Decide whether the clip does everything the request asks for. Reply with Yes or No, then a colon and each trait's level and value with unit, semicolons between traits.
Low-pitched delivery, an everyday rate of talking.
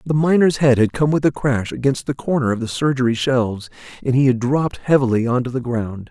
No: low, 130 Hz; fast, 235 wpm